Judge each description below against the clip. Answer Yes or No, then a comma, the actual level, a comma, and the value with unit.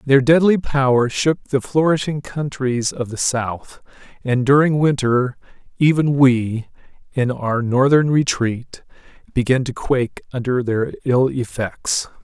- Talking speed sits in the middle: No, slow, 130 wpm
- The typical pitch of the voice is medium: No, low, 130 Hz